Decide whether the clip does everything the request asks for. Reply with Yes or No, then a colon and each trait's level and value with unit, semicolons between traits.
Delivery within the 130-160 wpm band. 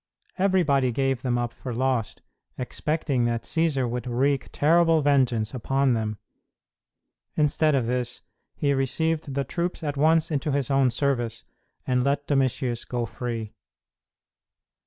Yes: slow, 135 wpm